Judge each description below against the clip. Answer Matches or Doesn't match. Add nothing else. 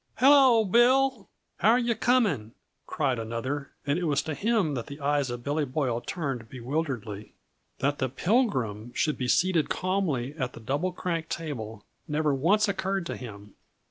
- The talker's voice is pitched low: Doesn't match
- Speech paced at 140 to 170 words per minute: Matches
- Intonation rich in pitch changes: Matches